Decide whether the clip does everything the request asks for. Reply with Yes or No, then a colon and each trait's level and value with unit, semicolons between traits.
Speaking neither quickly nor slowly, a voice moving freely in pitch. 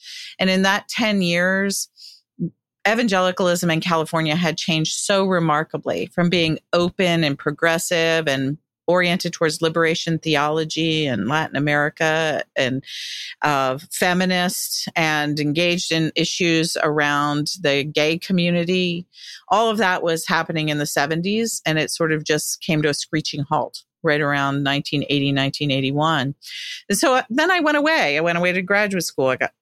No: average, 150 wpm; average, 3.3 semitones